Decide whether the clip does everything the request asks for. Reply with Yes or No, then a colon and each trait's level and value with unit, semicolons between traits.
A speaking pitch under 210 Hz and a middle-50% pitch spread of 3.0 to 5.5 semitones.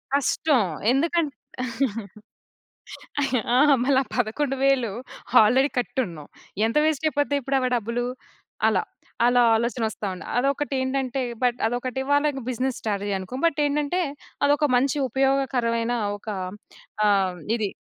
No: very high, 260 Hz; average, 3.4 semitones